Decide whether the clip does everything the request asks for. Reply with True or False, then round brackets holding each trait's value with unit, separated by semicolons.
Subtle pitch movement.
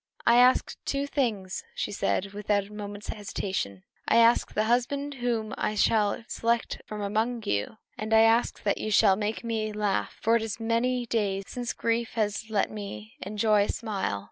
True (2.3 semitones)